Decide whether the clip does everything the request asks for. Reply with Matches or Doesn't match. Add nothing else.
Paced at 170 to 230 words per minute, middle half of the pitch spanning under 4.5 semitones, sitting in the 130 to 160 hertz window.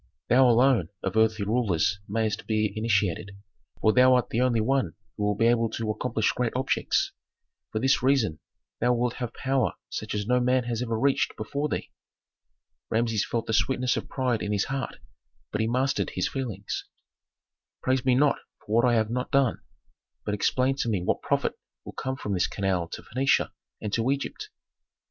Doesn't match